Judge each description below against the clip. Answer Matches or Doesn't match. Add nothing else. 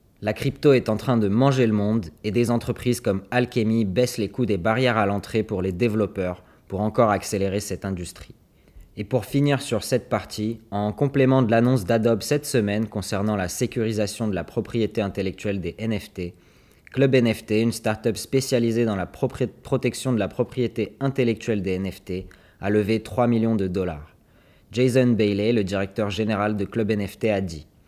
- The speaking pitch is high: Doesn't match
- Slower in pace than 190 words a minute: Matches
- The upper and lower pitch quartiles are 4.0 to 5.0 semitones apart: Doesn't match